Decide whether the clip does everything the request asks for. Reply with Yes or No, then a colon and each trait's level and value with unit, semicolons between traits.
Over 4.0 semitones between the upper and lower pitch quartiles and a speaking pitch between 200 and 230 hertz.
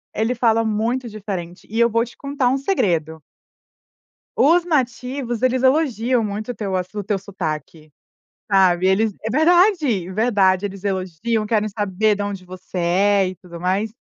Yes: average, 4.5 semitones; high, 210 Hz